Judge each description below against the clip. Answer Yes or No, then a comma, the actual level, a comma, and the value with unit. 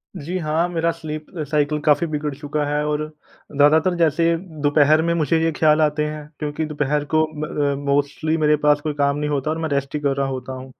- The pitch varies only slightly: Yes, narrow, 1.4 semitones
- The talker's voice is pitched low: No, medium, 150 Hz